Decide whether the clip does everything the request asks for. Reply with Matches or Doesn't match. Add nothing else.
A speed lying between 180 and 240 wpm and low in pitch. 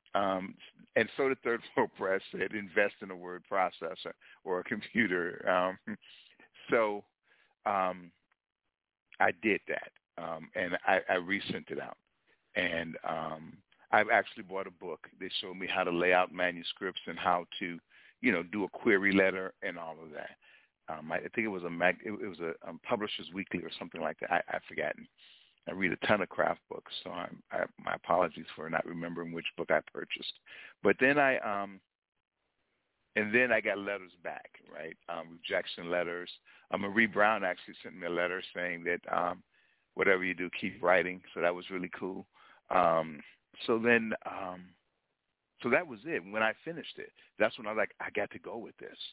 Matches